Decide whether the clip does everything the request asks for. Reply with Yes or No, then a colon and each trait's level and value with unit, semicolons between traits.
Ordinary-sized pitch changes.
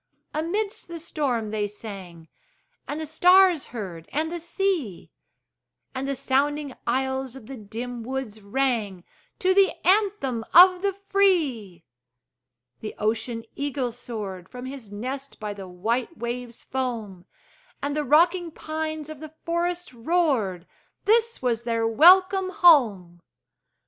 No: wide, 7.2 semitones